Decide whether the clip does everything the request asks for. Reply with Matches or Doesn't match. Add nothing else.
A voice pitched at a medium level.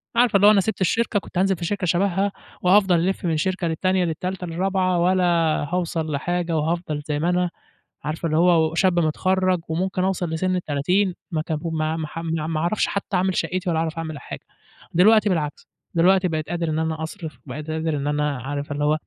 Matches